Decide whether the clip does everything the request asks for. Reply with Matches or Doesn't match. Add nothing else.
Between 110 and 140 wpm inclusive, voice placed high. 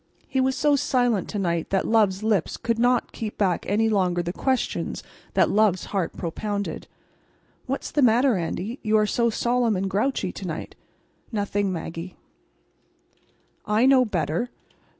Doesn't match